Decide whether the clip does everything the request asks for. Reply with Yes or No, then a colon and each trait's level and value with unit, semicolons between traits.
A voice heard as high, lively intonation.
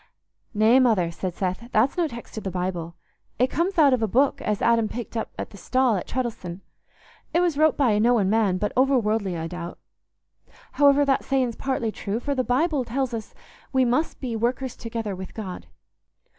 No: high, 235 Hz; average, 4.5 semitones